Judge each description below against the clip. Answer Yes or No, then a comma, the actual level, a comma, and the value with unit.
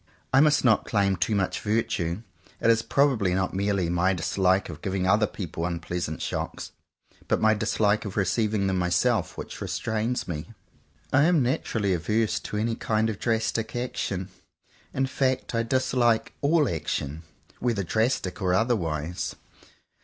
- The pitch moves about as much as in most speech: Yes, average, 4.1 semitones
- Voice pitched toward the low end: Yes, low, 105 Hz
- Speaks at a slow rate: No, average, 150 wpm